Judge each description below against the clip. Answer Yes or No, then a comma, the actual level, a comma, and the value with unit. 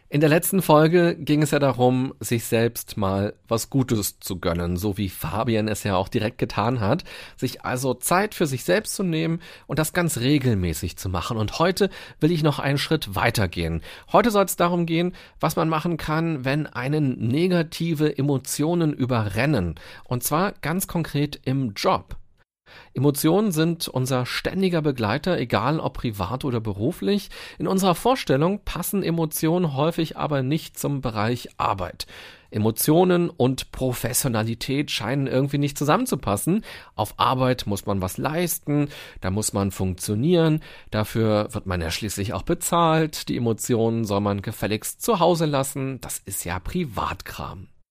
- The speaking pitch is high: No, low, 135 Hz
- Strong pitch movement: Yes, wide, 7.0 semitones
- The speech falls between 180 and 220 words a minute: No, average, 155 wpm